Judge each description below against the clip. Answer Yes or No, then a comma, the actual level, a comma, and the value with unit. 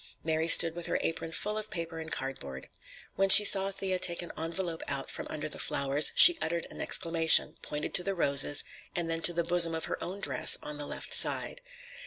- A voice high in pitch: No, medium, 165 Hz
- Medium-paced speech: No, fast, 215 wpm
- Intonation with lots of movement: No, narrow, 2.4 semitones